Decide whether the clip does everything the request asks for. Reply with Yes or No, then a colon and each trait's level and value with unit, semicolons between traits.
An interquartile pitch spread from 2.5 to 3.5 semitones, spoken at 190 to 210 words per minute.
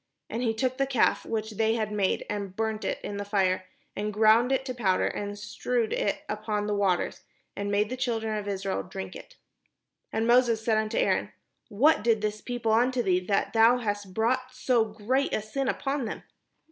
Yes: average, 2.9 semitones; average, 200 wpm